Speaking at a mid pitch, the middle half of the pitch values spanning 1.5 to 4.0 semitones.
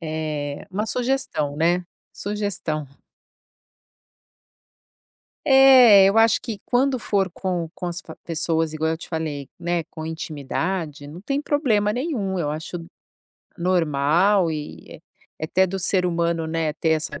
No: medium, 175 Hz; average, 4.4 semitones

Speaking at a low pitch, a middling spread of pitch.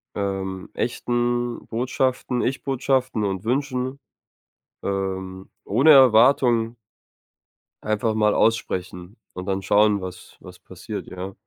Yes: low, 110 Hz; average, 4.6 semitones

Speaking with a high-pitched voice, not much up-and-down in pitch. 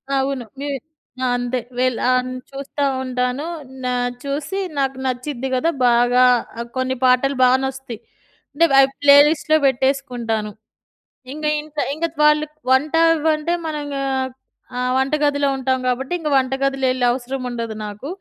Yes: very high, 265 Hz; narrow, 2.3 semitones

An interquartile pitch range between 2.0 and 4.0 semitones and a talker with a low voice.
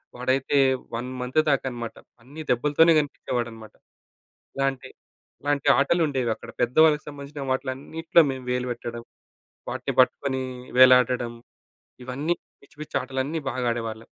Yes: average, 2.8 semitones; low, 130 Hz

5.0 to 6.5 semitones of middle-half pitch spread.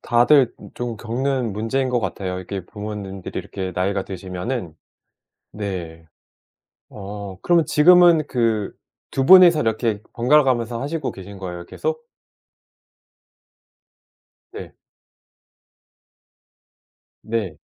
Yes: wide, 5.5 semitones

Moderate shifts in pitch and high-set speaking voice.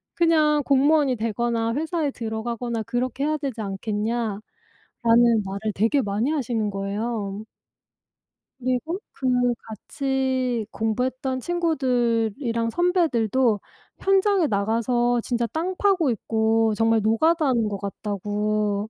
Yes: average, 3.9 semitones; high, 235 Hz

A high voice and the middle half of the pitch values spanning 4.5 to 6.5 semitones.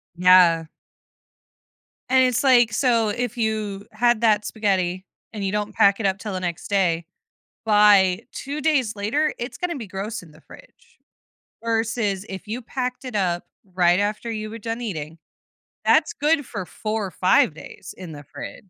No: high, 210 Hz; average, 3.9 semitones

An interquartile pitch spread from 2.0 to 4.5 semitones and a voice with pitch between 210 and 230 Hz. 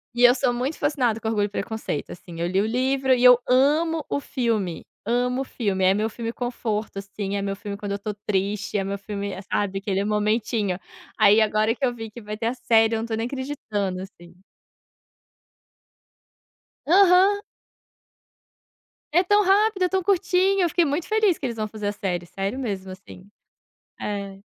No: average, 4.9 semitones; high, 220 Hz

